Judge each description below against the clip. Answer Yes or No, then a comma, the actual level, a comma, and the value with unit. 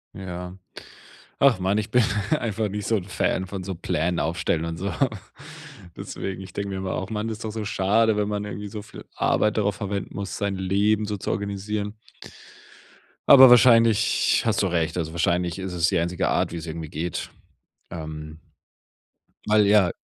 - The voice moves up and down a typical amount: Yes, average, 3.1 semitones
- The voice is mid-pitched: No, low, 100 Hz